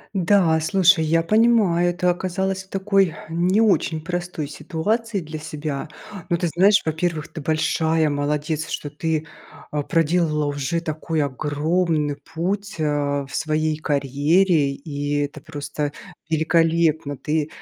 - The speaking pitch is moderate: Yes, medium, 160 Hz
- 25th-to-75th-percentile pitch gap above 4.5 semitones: No, average, 3.0 semitones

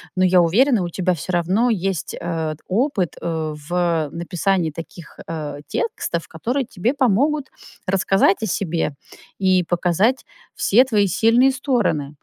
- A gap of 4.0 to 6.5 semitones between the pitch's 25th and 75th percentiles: Yes, wide, 5.5 semitones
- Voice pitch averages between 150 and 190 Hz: Yes, medium, 185 Hz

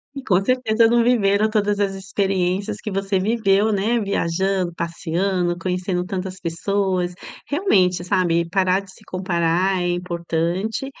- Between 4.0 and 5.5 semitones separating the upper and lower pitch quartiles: No, narrow, 2.4 semitones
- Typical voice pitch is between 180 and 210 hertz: Yes, high, 190 Hz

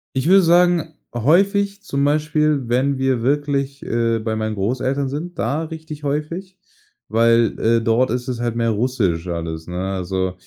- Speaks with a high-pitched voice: No, low, 130 Hz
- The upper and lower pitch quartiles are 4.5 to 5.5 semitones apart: Yes, average, 5.1 semitones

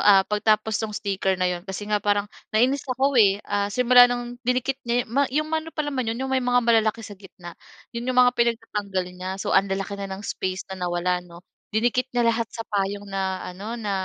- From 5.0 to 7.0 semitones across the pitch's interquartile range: No, average, 4.1 semitones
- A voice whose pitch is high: Yes, high, 215 Hz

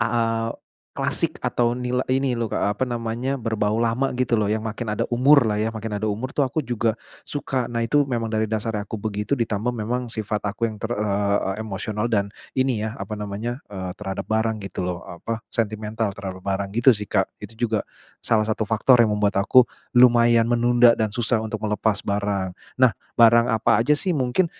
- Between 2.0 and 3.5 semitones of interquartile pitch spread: Yes, narrow, 2.5 semitones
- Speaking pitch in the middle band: No, low, 110 Hz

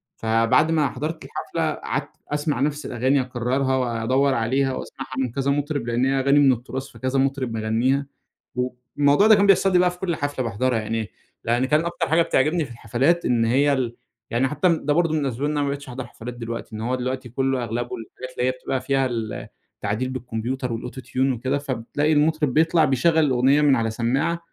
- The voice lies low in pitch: Yes, low, 130 Hz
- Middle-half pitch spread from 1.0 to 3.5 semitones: Yes, average, 3.2 semitones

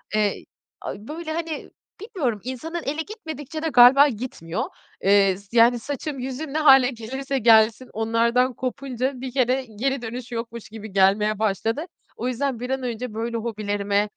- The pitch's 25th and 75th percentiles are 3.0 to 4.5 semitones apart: Yes, average, 3.7 semitones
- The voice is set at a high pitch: Yes, high, 245 Hz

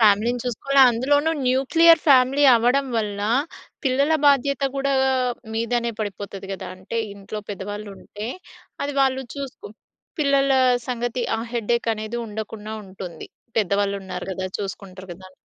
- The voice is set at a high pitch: Yes, high, 230 Hz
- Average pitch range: Yes, average, 5.0 semitones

